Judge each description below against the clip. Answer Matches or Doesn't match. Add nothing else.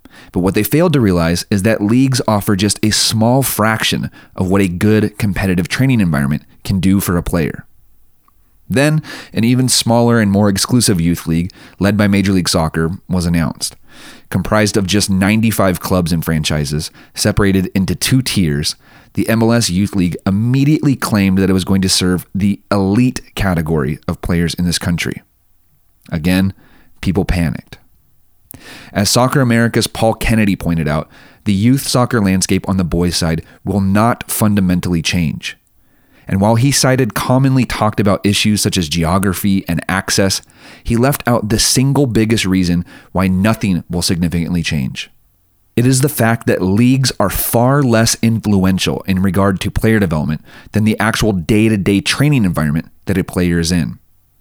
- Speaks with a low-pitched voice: Matches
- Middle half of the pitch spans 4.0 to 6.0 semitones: Matches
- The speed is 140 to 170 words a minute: Matches